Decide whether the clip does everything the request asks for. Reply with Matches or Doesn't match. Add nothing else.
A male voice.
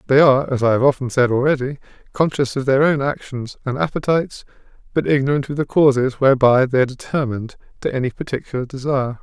Matches